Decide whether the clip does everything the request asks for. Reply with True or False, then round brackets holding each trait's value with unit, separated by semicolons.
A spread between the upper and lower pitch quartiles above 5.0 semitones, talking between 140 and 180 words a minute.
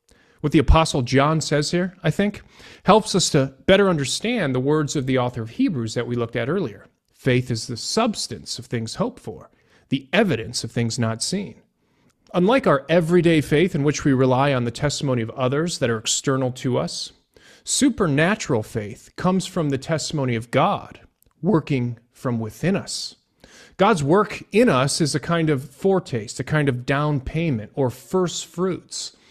True (5.6 semitones; 175 wpm)